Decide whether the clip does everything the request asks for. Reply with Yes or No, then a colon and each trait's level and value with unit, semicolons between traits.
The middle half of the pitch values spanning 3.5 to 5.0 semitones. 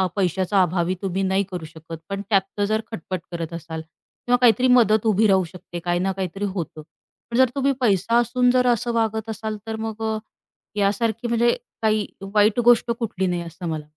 Yes: average, 4.0 semitones